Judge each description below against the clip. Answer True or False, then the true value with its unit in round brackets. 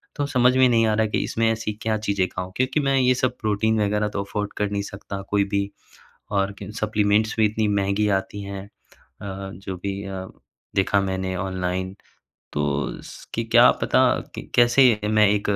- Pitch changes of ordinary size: False (2.1 semitones)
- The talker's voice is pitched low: True (105 Hz)